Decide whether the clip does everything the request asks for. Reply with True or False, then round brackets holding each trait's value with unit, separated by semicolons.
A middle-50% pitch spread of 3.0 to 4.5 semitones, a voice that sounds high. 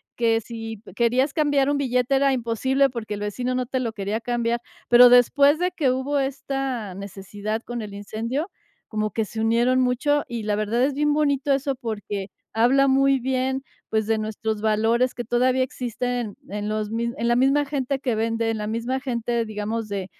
True (3.3 semitones; 240 Hz)